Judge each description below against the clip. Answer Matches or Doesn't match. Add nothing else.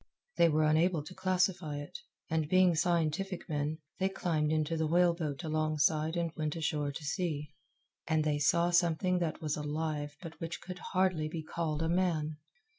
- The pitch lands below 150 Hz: Doesn't match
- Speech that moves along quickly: Doesn't match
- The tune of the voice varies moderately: Doesn't match